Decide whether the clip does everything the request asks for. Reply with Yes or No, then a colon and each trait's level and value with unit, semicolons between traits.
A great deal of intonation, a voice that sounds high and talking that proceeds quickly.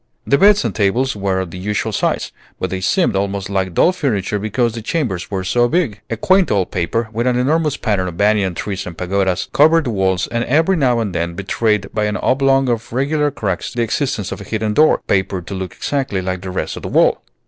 No: wide, 5.8 semitones; low, 105 Hz; fast, 225 wpm